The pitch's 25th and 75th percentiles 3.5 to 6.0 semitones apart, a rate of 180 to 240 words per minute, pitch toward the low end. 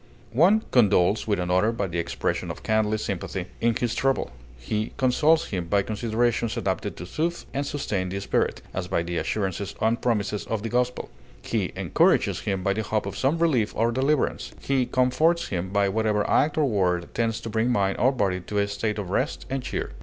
Yes: average, 4.3 semitones; average, 200 wpm; low, 110 Hz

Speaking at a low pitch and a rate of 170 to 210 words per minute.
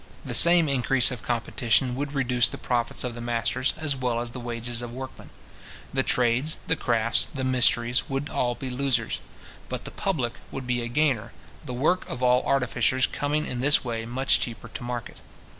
Yes: low, 125 Hz; average, 190 wpm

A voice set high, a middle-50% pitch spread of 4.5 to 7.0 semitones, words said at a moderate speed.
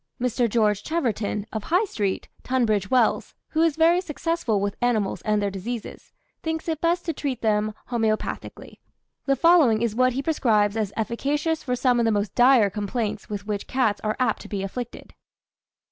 Yes: high, 235 Hz; average, 4.8 semitones; average, 175 wpm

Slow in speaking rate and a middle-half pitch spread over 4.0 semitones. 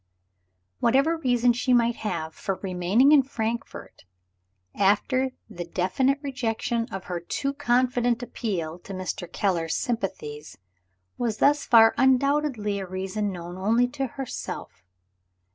Yes: slow, 125 wpm; wide, 5.4 semitones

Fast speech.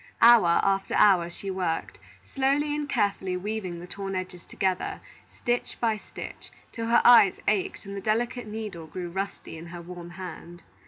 No: average, 165 wpm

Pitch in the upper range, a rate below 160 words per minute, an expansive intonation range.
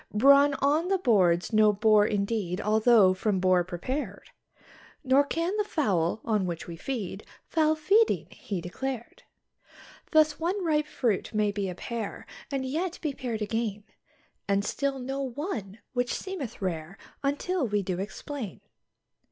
Yes: high, 230 Hz; average, 145 wpm; wide, 6.4 semitones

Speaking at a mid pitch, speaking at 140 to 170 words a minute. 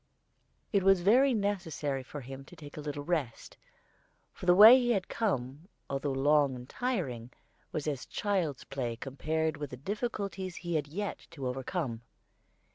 Yes: medium, 155 Hz; average, 160 wpm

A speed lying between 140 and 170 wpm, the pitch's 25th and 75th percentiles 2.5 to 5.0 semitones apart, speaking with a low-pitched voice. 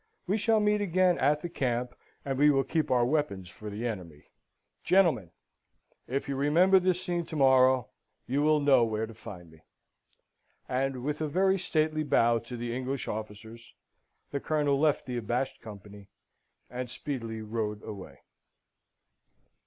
No: average, 155 wpm; wide, 5.4 semitones; low, 130 Hz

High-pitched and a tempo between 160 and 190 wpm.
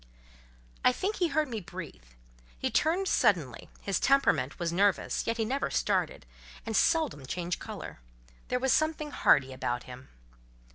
No: high, 215 Hz; average, 150 wpm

